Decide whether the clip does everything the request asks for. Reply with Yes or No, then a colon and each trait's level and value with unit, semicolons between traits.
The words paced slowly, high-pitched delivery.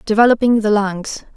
Yes: slow, 130 wpm; high, 215 Hz